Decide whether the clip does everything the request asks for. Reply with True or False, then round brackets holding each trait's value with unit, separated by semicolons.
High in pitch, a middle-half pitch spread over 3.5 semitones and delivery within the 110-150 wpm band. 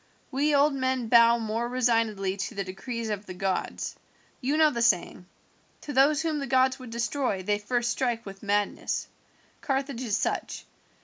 False (235 Hz; 4.3 semitones; 165 wpm)